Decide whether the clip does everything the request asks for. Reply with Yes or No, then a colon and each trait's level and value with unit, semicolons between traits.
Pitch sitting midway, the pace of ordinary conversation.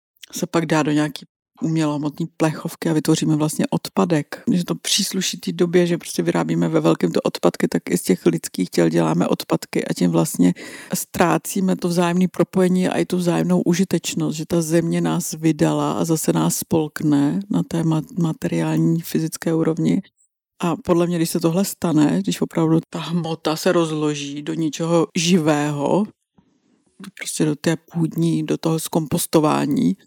Yes: medium, 165 Hz; average, 160 wpm